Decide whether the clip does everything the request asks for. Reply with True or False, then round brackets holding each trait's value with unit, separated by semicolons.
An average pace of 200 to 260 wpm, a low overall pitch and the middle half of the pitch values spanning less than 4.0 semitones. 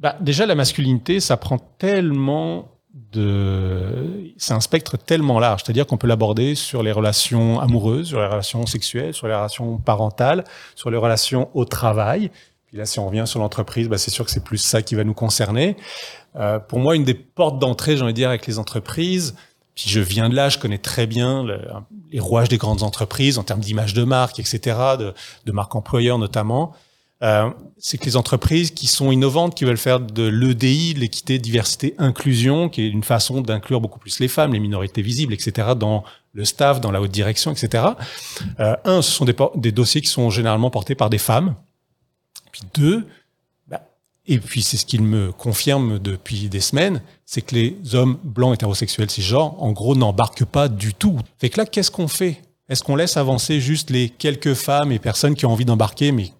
False (205 wpm; 120 Hz; 4.4 semitones)